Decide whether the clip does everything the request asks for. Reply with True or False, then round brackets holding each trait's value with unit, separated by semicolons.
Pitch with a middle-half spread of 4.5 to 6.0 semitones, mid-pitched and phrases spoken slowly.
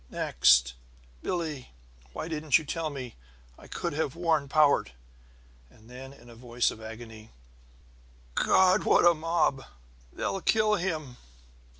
True (5.6 semitones; 145 Hz; 130 wpm)